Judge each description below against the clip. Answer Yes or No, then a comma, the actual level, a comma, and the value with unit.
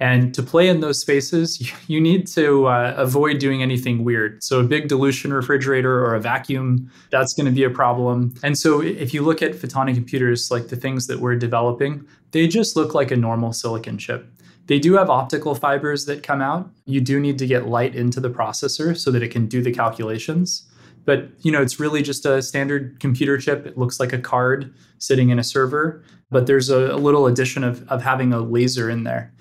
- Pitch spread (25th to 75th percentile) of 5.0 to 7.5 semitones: No, average, 2.8 semitones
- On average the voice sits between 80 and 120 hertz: No, low, 135 Hz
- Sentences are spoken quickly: Yes, fast, 215 wpm